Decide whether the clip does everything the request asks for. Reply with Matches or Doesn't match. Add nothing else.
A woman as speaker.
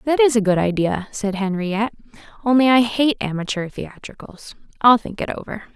Matches